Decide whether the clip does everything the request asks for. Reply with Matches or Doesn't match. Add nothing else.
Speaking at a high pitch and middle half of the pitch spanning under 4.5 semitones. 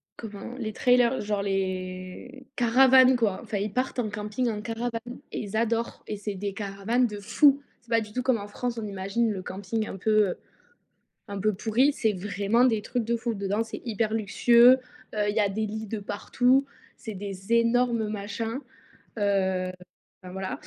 Matches